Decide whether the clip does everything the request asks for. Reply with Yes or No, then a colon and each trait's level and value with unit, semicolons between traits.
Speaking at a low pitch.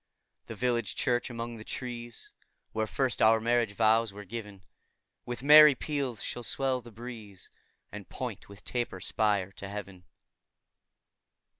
Yes: low, 115 Hz